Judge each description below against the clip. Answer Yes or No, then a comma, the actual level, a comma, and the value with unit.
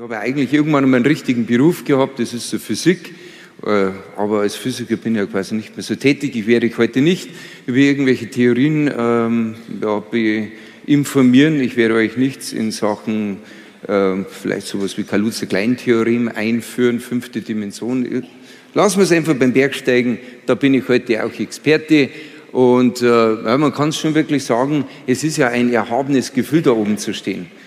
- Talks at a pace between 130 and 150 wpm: No, average, 170 wpm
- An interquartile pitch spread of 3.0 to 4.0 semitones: Yes, average, 3.6 semitones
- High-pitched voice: No, low, 120 Hz